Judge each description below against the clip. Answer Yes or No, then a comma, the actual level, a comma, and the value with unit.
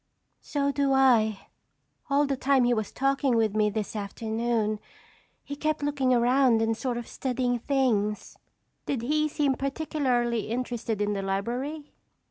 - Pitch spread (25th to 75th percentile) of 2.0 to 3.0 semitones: No, average, 3.8 semitones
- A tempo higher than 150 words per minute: No, average, 145 wpm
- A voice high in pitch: Yes, high, 245 Hz